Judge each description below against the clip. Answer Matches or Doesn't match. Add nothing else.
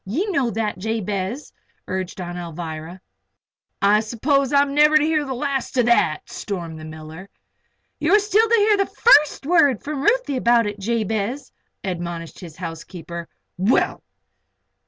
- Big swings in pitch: Matches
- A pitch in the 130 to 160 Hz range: Doesn't match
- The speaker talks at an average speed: Matches